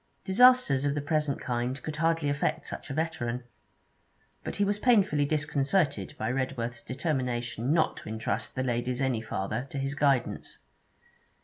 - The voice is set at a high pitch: No, medium, 140 Hz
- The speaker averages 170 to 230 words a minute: No, average, 150 wpm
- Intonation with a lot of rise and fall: No, average, 4.2 semitones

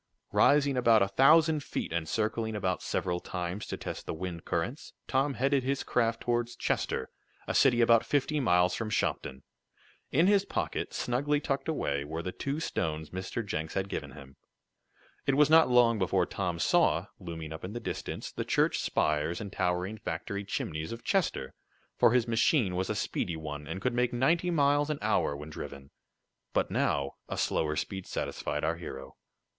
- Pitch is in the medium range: No, low, 105 Hz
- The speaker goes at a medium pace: Yes, average, 180 wpm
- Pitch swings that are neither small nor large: No, wide, 8.2 semitones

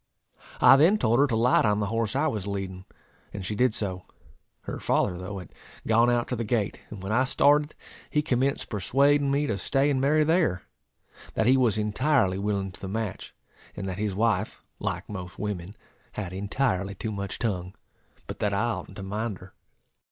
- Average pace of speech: Yes, average, 195 wpm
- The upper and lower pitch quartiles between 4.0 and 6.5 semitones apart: Yes, average, 5.0 semitones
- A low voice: Yes, low, 110 Hz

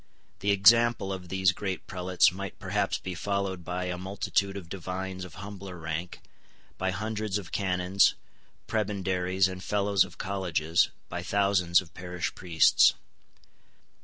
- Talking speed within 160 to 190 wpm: No, slow, 135 wpm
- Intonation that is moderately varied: No, narrow, 1.7 semitones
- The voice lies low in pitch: Yes, very low, 95 Hz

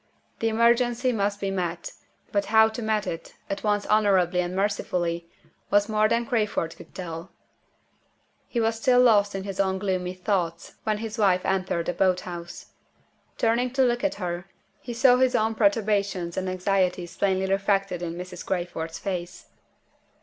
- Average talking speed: Yes, average, 165 wpm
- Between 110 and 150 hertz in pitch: No, high, 195 Hz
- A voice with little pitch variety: No, average, 3.5 semitones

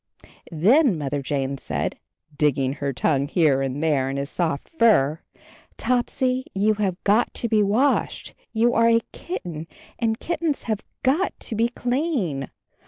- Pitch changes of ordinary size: No, wide, 9.0 semitones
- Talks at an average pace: Yes, average, 150 wpm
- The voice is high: Yes, high, 200 Hz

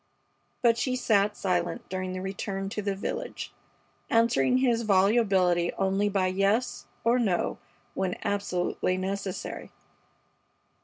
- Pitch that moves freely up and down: No, average, 3.0 semitones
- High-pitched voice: Yes, high, 195 Hz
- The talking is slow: Yes, slow, 115 wpm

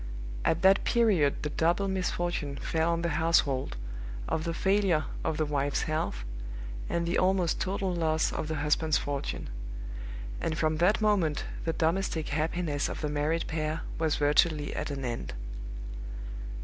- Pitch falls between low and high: Yes, medium, 160 Hz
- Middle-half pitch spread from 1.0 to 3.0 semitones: Yes, average, 2.7 semitones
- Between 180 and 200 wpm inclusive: No, average, 150 wpm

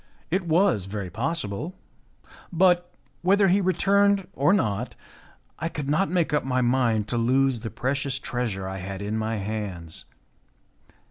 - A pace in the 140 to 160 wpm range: Yes, average, 145 wpm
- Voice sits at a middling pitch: No, low, 130 Hz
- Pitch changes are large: Yes, wide, 8.5 semitones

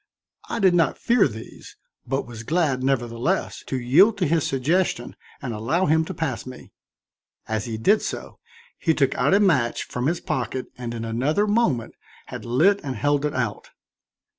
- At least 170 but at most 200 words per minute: Yes, average, 175 wpm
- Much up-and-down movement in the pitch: Yes, wide, 6.1 semitones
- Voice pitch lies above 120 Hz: Yes, low, 135 Hz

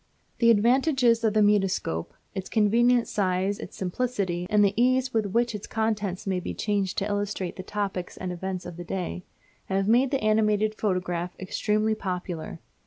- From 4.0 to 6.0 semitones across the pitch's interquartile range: No, average, 3.2 semitones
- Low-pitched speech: No, high, 205 Hz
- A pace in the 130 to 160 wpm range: No, average, 170 wpm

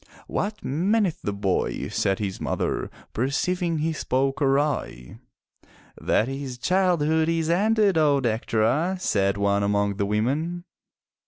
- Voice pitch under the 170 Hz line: Yes, medium, 140 Hz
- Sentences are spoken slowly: Yes, slow, 120 wpm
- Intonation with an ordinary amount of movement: No, wide, 8.1 semitones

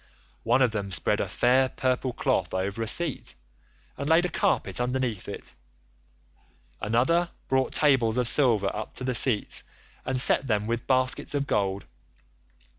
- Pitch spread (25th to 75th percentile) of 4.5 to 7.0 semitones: No, average, 3.4 semitones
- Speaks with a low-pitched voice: Yes, low, 125 Hz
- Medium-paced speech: Yes, average, 155 wpm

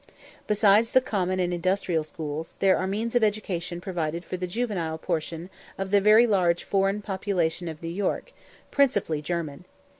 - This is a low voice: No, medium, 185 Hz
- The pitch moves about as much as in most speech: Yes, average, 3.4 semitones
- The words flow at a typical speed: Yes, average, 160 wpm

